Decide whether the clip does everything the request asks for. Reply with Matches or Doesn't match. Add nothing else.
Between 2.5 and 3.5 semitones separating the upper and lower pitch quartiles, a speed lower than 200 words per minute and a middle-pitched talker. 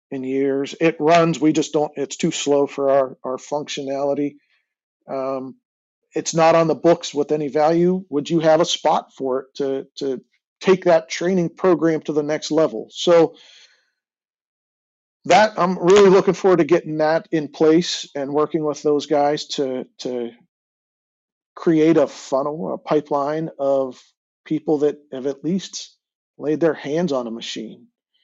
Matches